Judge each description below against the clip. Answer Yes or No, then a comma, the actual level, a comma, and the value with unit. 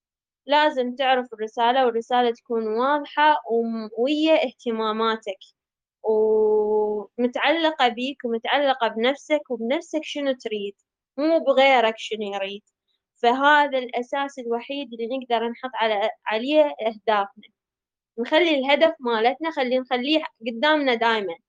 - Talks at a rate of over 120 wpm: No, average, 100 wpm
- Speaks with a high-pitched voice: Yes, high, 245 Hz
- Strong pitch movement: No, average, 4.0 semitones